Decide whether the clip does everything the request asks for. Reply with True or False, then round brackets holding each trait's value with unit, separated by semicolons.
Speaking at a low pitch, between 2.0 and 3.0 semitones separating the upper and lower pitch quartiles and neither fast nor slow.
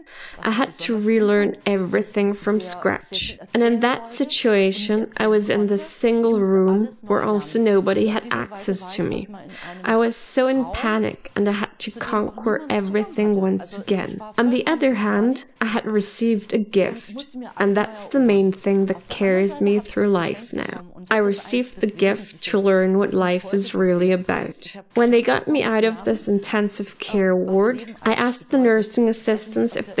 False (210 Hz; 2.5 semitones; 170 wpm)